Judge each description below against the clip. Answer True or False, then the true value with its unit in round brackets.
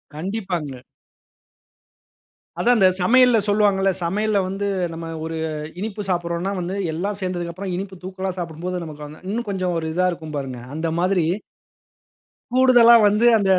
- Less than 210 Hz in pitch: True (185 Hz)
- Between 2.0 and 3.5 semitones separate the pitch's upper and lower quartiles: True (3.2 semitones)